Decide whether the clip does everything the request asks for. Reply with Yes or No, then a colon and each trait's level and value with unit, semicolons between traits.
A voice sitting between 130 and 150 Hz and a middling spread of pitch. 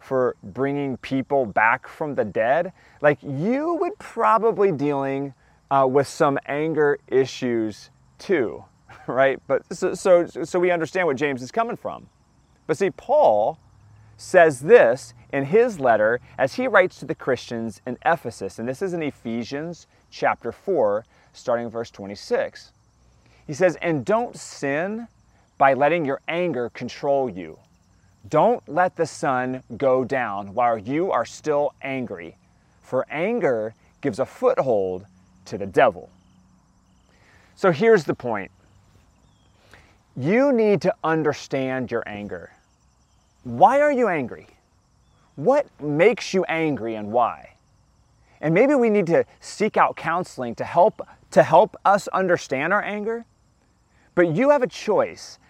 No: medium, 140 Hz; wide, 8.1 semitones